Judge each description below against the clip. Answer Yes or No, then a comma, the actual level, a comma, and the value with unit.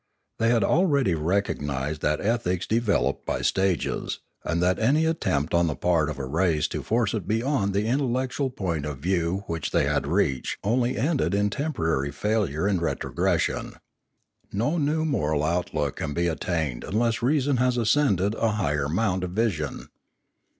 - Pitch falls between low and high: No, very low, 95 Hz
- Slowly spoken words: No, average, 165 wpm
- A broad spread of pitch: Yes, wide, 6.8 semitones